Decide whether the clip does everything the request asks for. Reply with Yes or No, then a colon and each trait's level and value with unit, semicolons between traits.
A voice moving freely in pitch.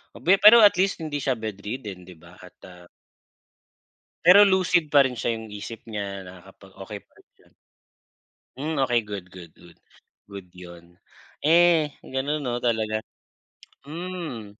Yes: wide, 8.2 semitones